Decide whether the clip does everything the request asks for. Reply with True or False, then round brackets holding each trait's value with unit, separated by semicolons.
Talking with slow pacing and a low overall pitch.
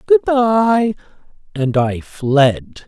False (105 wpm; 185 Hz)